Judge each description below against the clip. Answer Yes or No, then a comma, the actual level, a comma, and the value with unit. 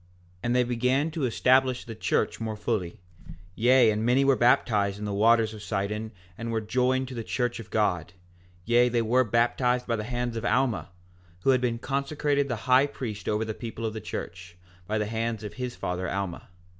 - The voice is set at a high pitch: No, low, 115 Hz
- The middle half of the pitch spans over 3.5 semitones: No, average, 2.9 semitones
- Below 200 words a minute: No, fast, 205 wpm